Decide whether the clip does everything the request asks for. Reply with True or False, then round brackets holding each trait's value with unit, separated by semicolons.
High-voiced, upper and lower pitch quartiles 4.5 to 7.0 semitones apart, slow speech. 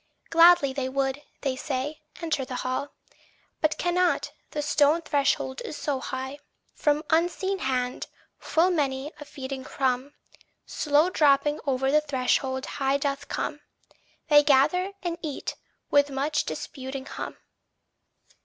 False (285 Hz; 2.5 semitones; 130 wpm)